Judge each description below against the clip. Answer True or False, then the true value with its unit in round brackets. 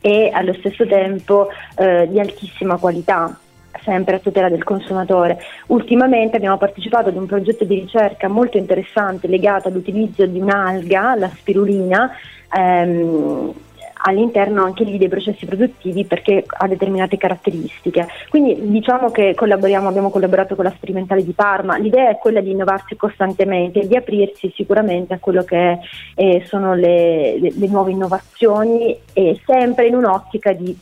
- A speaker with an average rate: True (150 wpm)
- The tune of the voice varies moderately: False (2.0 semitones)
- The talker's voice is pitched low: False (195 Hz)